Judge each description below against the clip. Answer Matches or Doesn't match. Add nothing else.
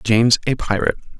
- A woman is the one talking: Doesn't match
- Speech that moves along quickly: Doesn't match